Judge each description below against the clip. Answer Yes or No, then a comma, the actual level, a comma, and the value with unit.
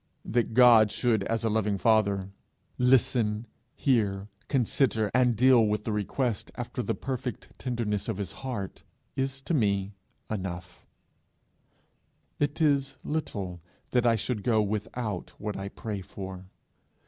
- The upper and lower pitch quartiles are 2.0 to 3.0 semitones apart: No, average, 3.7 semitones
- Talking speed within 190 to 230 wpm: No, slow, 135 wpm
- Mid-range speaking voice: No, low, 110 Hz